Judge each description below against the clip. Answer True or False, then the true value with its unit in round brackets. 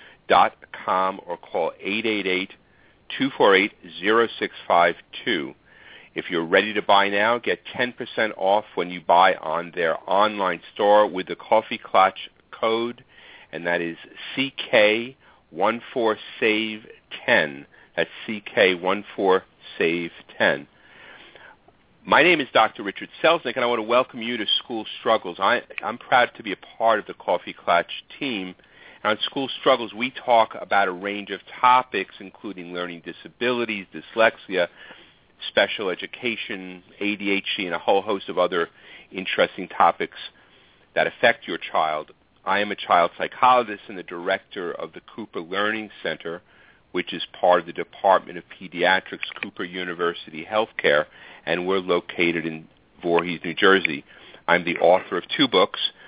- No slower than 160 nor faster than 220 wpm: False (135 wpm)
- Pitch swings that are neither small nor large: True (4.4 semitones)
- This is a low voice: True (100 Hz)